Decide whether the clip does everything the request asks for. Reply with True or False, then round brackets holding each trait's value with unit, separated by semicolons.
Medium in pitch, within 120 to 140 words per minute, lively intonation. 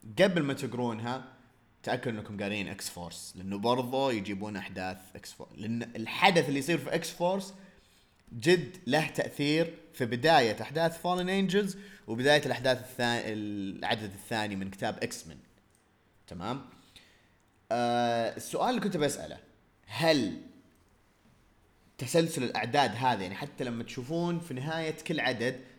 False (125 Hz; 130 wpm; 6.8 semitones)